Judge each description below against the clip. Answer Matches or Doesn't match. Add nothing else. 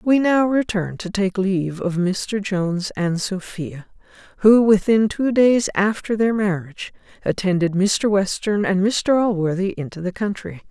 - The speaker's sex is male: Doesn't match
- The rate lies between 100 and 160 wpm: Matches